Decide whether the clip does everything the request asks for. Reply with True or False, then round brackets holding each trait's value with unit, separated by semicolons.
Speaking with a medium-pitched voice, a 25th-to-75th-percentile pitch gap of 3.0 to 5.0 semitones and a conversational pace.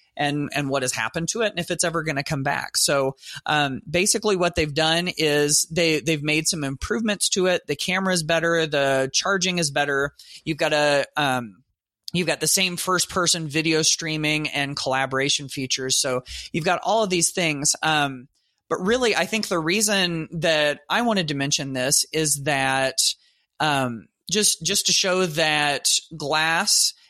True (155 Hz; 4.0 semitones; 175 wpm)